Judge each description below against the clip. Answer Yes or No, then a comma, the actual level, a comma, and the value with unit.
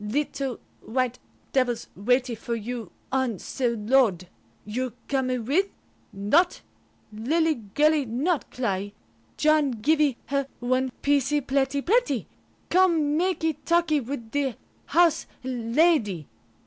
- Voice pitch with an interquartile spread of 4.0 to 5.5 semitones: Yes, average, 4.5 semitones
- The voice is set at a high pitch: Yes, very high, 265 Hz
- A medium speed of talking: No, slow, 110 wpm